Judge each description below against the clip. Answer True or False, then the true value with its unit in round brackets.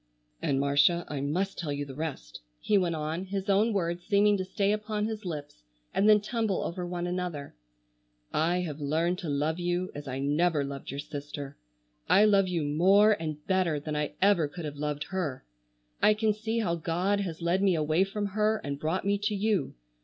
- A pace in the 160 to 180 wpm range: False (200 wpm)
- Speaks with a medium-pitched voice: True (175 Hz)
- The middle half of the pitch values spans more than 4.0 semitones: True (4.9 semitones)